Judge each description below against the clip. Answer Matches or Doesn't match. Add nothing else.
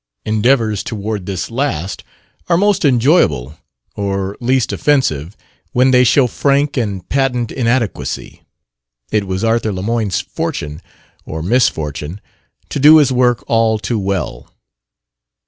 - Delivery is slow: Matches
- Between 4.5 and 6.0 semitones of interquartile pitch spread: Matches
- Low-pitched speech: Matches